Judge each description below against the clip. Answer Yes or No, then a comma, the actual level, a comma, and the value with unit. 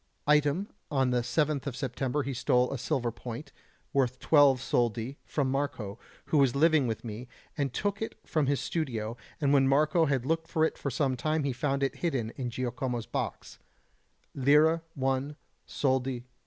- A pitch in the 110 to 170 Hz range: Yes, low, 135 Hz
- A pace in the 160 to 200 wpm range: Yes, average, 175 wpm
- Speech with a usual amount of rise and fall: Yes, average, 3.1 semitones